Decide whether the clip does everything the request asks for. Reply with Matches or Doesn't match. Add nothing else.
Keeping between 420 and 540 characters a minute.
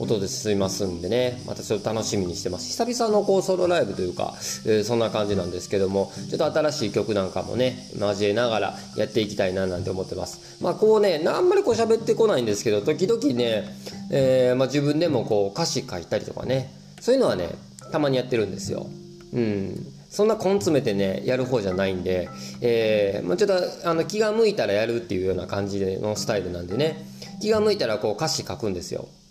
Matches